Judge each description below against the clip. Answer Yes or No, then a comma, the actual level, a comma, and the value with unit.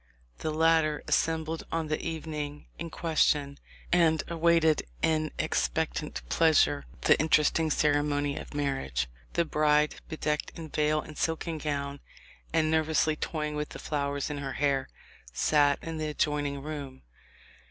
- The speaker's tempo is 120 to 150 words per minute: Yes, average, 145 wpm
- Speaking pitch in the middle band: Yes, medium, 150 Hz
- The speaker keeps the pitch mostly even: Yes, narrow, 1.7 semitones